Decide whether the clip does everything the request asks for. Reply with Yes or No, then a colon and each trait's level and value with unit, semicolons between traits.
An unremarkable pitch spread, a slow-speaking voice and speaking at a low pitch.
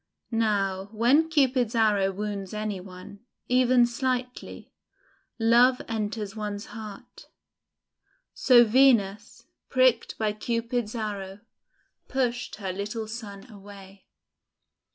No: average, 3.2 semitones; slow, 95 wpm; high, 220 Hz